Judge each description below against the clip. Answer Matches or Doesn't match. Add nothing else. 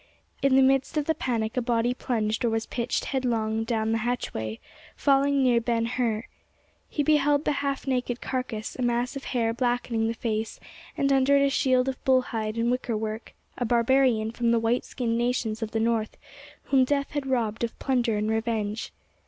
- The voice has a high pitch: Matches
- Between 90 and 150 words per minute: Doesn't match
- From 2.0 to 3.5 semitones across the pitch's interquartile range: Matches